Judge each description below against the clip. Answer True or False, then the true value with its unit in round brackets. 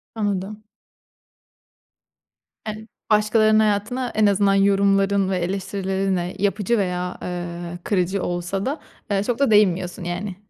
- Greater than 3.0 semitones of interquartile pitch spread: False (2.6 semitones)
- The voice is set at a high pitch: True (195 Hz)